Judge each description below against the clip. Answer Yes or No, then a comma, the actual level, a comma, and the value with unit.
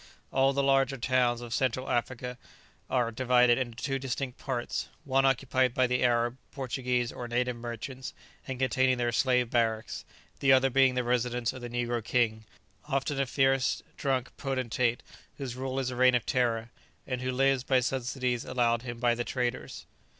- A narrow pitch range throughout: Yes, narrow, 1.6 semitones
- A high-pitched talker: No, low, 125 Hz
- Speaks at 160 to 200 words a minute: Yes, average, 170 wpm